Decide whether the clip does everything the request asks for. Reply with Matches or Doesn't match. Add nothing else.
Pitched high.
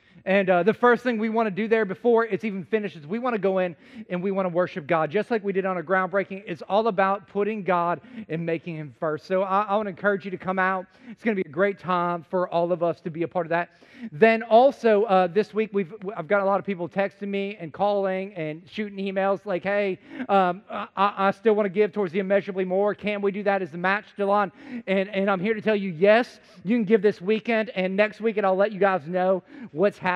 Matches